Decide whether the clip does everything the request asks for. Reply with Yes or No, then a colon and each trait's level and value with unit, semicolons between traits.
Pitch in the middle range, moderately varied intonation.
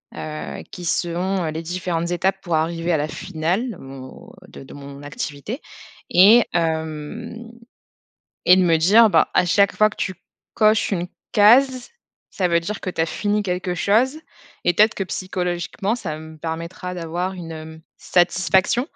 Yes: medium, 175 Hz; average, 3.7 semitones